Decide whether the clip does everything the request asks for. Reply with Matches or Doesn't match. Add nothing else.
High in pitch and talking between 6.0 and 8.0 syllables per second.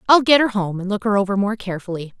Matches